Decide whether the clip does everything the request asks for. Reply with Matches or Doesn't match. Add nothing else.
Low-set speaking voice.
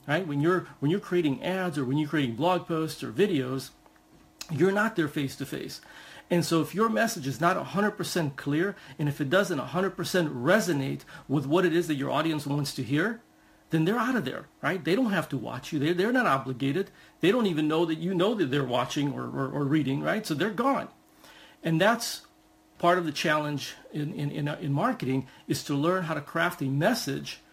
Doesn't match